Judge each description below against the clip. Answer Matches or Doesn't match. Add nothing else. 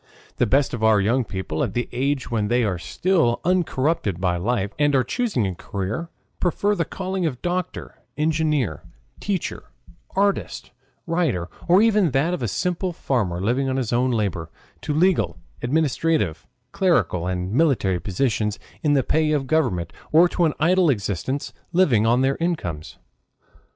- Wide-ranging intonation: Matches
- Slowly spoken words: Doesn't match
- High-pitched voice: Doesn't match